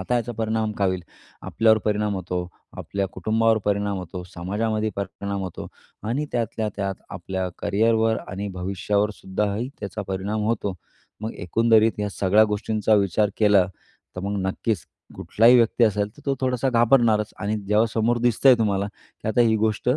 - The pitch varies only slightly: Yes, narrow, 2.3 semitones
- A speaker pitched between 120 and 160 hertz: No, low, 105 Hz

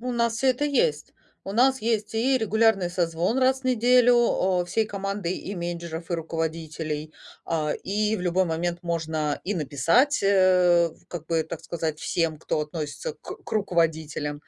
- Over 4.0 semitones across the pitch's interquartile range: Yes, average, 5.3 semitones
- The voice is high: No, medium, 175 Hz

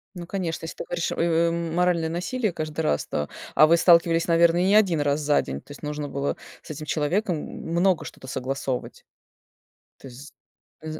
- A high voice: No, medium, 165 Hz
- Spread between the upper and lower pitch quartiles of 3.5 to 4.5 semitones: No, average, 2.8 semitones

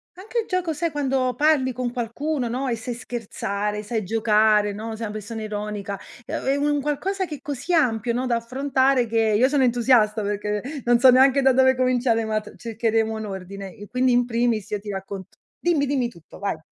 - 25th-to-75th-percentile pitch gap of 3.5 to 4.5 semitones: Yes, average, 4.0 semitones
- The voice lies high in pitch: Yes, high, 240 Hz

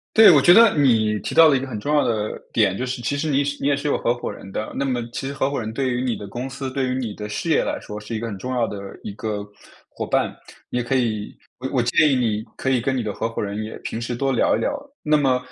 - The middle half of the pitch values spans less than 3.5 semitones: No, average, 3.8 semitones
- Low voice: Yes, low, 125 Hz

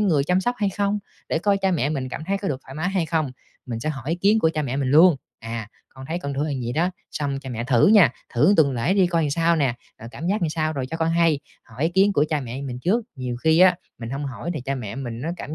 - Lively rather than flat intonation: No, average, 4.9 semitones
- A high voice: No, medium, 155 Hz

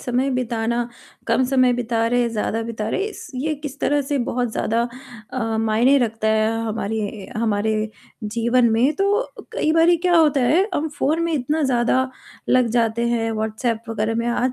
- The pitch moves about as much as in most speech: Yes, average, 3.6 semitones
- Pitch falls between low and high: No, high, 240 Hz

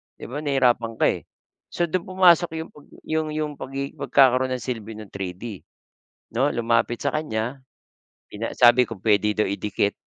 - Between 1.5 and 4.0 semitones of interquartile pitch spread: No, average, 5.1 semitones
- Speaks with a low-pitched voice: Yes, low, 125 Hz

